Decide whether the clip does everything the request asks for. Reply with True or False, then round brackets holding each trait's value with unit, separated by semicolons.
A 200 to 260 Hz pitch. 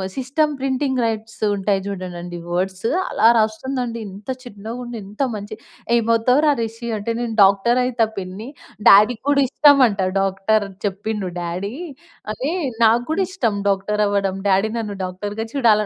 True (220 Hz)